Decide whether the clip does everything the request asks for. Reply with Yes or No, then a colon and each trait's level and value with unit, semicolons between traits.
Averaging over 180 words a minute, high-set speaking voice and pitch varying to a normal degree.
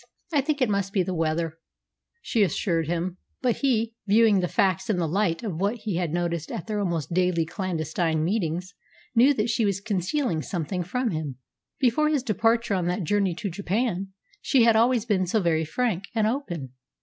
Yes: average, 190 wpm; high, 195 Hz; average, 5.0 semitones